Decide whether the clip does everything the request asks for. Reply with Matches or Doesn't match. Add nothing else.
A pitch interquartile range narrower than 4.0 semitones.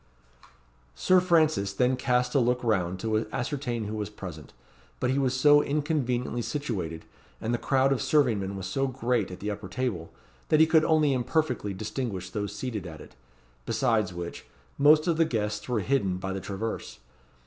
Doesn't match